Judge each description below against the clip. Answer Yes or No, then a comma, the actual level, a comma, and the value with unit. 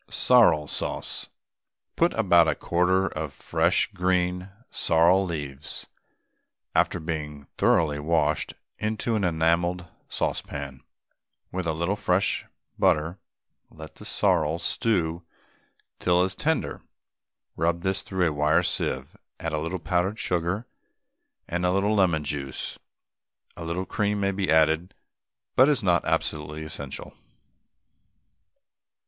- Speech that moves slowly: Yes, slow, 125 wpm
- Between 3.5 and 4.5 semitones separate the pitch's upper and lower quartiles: No, average, 3.1 semitones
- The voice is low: Yes, very low, 85 Hz